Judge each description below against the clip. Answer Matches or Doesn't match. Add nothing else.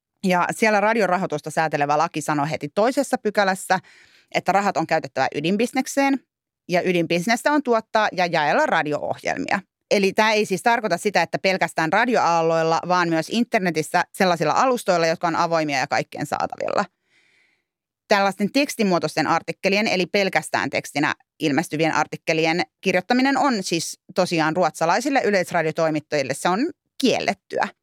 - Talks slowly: Doesn't match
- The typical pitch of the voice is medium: Matches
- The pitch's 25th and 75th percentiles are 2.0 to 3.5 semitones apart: Doesn't match